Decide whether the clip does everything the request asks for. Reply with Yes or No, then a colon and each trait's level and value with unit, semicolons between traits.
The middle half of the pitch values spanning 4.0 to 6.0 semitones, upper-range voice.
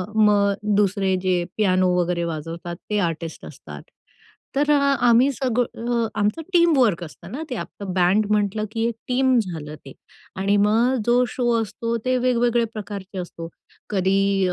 Yes: average, 4.5 semitones; high, 210 Hz